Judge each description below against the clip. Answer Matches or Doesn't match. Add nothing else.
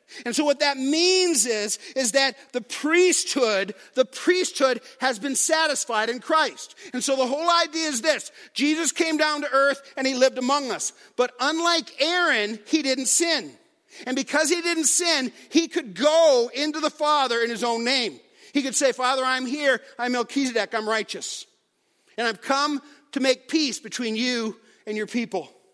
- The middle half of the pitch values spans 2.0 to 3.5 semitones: Doesn't match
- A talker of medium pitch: Doesn't match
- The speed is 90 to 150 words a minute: Doesn't match